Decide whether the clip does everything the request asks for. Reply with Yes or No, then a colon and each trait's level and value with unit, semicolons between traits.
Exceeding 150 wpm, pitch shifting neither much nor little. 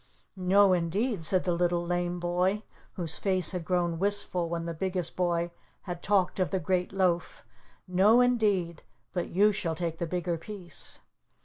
No: average, 165 wpm; narrow, 2.1 semitones